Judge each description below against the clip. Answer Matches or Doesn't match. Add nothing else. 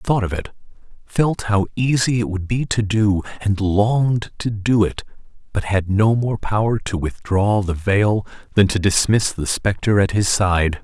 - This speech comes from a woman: Doesn't match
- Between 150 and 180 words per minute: Doesn't match